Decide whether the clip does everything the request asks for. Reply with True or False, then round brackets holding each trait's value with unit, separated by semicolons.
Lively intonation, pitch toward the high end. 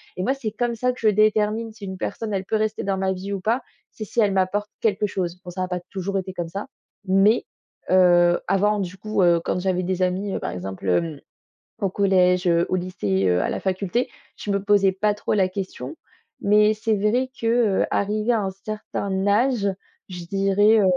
False (2.5 semitones; 195 Hz)